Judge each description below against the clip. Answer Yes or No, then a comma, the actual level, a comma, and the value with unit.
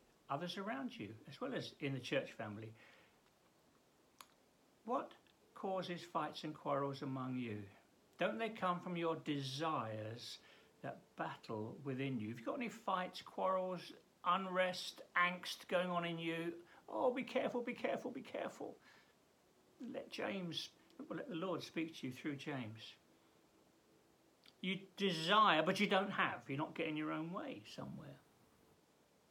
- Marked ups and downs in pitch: Yes, wide, 5.9 semitones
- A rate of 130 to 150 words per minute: Yes, average, 145 wpm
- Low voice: No, medium, 165 Hz